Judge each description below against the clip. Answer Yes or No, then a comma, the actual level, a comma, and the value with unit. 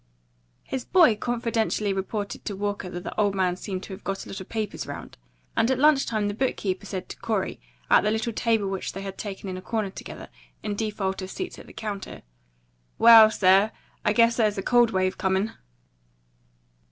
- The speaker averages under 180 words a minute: No, average, 200 wpm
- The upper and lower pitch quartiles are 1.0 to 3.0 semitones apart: Yes, average, 2.7 semitones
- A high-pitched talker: Yes, high, 205 Hz